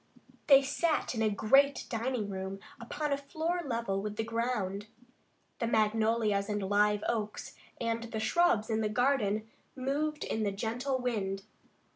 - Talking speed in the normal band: Yes, average, 150 wpm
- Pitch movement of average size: Yes, average, 3.9 semitones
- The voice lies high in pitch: Yes, high, 225 Hz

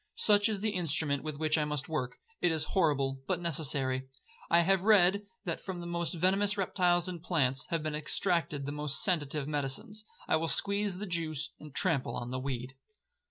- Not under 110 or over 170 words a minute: No, average, 185 wpm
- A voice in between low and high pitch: Yes, medium, 160 Hz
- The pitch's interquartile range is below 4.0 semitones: No, average, 4.4 semitones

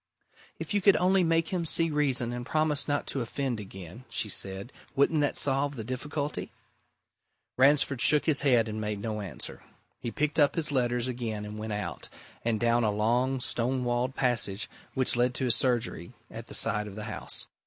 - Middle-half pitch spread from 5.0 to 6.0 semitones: No, average, 4.5 semitones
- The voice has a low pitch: Yes, low, 125 Hz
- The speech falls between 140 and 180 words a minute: No, average, 190 wpm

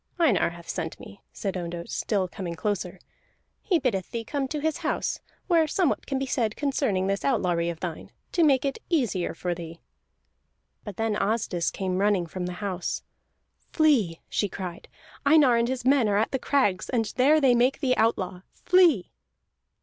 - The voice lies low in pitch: No, high, 215 Hz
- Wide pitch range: Yes, wide, 6.9 semitones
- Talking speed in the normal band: Yes, average, 175 wpm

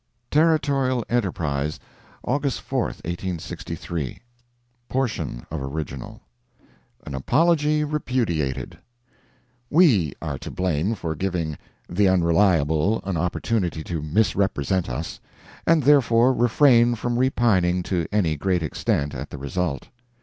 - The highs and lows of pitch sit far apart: Yes, wide, 7.5 semitones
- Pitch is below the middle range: Yes, very low, 95 Hz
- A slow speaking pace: Yes, slow, 105 wpm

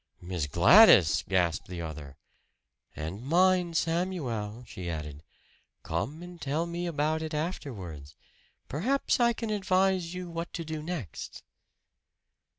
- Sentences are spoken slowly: Yes, slow, 125 wpm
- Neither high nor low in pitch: Yes, medium, 155 Hz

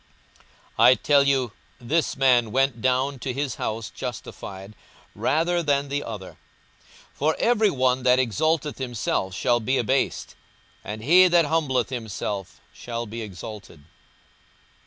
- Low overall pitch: Yes, low, 130 Hz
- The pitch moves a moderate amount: Yes, average, 4.1 semitones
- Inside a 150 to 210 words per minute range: No, slow, 135 wpm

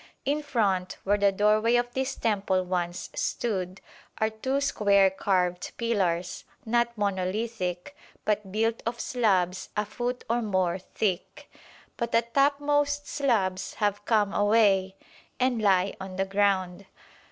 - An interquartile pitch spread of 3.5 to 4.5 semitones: Yes, average, 3.8 semitones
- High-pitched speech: Yes, high, 205 Hz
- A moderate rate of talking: No, slow, 130 wpm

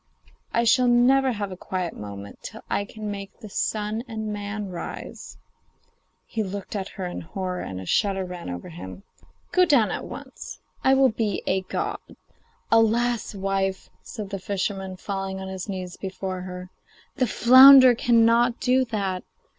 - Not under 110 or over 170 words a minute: Yes, average, 160 wpm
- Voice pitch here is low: No, high, 200 Hz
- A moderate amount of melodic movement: Yes, average, 3.7 semitones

